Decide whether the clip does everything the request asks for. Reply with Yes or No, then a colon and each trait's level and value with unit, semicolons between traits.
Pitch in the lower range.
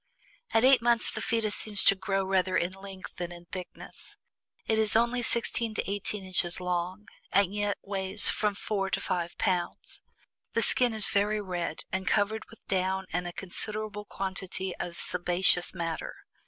No: high, 195 Hz